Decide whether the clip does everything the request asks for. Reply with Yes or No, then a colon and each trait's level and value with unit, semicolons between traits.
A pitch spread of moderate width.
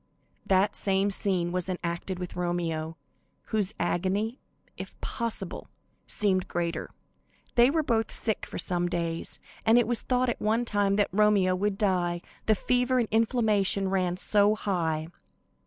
Yes: average, 3.7 semitones